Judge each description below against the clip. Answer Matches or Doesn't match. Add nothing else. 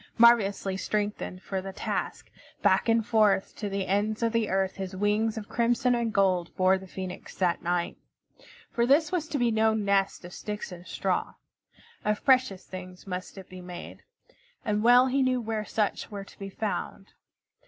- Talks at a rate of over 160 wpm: Matches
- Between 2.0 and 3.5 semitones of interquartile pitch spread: Matches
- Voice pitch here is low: Doesn't match